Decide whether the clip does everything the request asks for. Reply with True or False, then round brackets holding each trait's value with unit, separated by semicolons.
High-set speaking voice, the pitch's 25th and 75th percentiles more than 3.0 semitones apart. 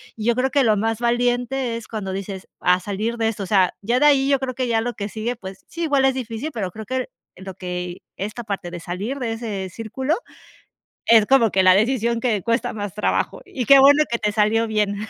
True (225 Hz; 3.7 semitones)